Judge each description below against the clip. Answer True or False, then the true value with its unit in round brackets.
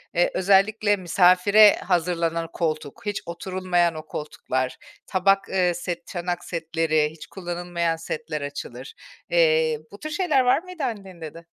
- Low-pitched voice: False (175 Hz)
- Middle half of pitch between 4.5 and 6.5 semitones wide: False (3.2 semitones)